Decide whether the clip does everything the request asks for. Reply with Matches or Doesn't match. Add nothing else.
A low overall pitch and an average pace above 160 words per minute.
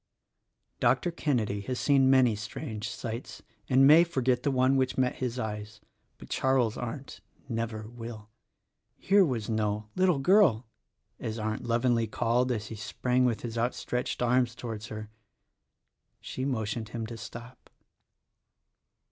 Doesn't match